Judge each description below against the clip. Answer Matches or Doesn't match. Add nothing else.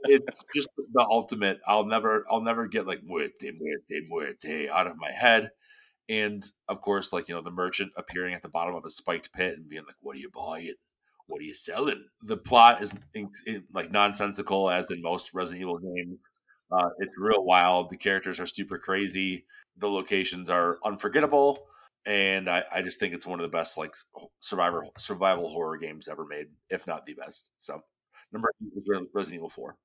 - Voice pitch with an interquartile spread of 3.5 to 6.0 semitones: Matches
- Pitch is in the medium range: Doesn't match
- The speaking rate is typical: Matches